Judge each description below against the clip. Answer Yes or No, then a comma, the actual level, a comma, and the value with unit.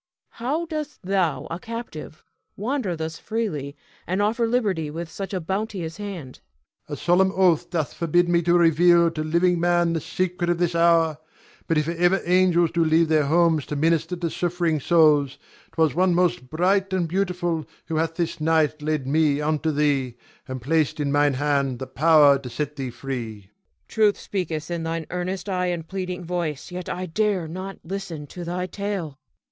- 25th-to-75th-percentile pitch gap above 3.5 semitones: No, average, 3.0 semitones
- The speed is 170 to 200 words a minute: Yes, average, 185 wpm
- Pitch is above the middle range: No, medium, 170 Hz